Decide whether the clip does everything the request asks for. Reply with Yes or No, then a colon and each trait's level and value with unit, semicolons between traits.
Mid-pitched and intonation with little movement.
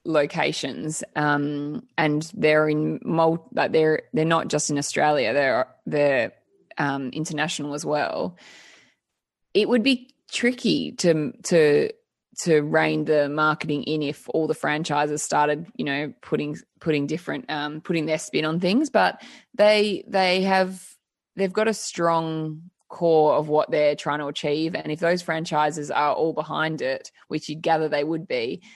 No: medium, 155 Hz; average, 3.5 semitones